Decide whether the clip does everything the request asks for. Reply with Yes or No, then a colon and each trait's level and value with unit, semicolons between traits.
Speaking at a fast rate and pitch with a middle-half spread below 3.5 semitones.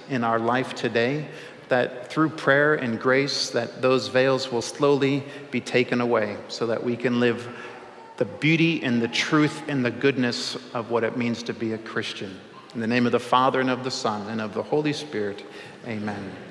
No: average, 195 wpm; average, 2.9 semitones